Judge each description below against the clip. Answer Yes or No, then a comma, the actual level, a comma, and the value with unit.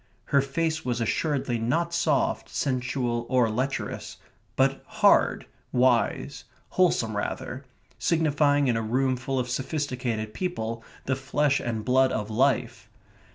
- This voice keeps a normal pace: No, slow, 125 wpm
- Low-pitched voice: Yes, low, 130 Hz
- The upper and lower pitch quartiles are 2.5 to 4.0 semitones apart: Yes, average, 3.1 semitones